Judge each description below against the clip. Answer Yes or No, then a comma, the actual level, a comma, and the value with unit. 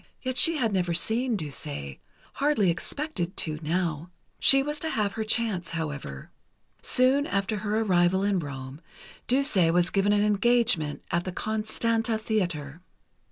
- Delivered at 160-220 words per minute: No, average, 145 wpm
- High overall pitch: Yes, high, 200 Hz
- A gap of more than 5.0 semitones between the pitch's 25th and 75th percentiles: Yes, wide, 5.5 semitones